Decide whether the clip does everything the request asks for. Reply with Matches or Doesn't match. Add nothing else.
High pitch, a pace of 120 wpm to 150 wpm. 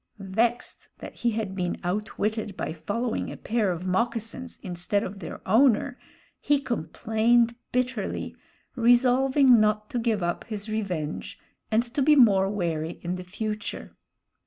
Matches